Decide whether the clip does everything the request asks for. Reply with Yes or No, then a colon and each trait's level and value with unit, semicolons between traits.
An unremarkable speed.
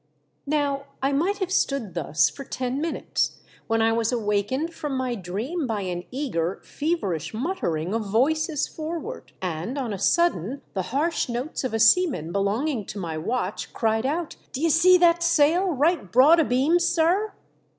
Yes: average, 170 wpm